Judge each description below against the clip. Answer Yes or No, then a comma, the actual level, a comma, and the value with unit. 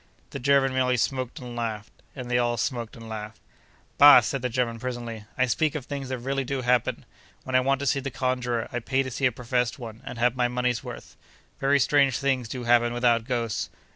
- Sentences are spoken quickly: Yes, fast, 220 wpm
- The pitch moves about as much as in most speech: No, narrow, 2.0 semitones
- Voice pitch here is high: No, low, 125 Hz